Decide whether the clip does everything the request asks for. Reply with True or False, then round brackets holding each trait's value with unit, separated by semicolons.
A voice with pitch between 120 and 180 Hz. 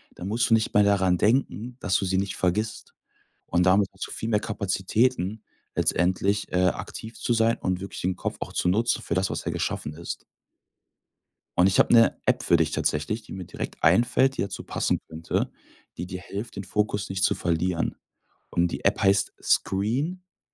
False (100 Hz)